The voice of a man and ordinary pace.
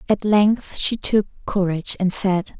No: female; average, 160 wpm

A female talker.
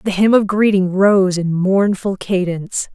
Yes: female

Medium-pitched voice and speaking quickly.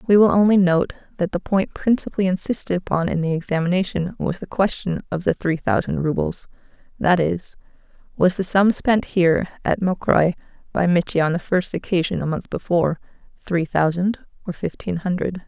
No: medium, 180 Hz; average, 170 wpm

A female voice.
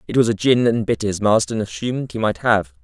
No: male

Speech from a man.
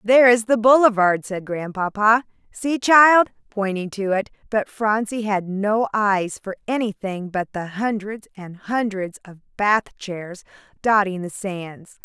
No: female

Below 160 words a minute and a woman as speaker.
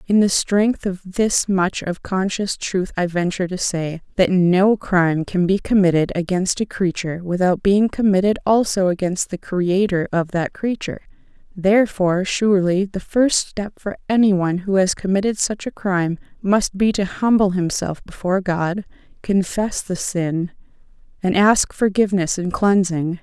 Yes: average, 150 wpm; female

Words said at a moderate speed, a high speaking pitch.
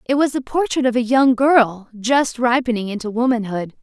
Yes: average, 190 wpm; high, 245 Hz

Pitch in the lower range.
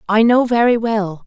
No: high, 220 Hz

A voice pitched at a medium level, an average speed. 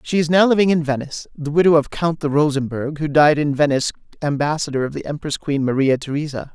No: medium, 150 Hz; fast, 210 wpm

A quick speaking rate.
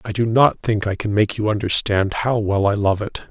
Yes: fast, 255 wpm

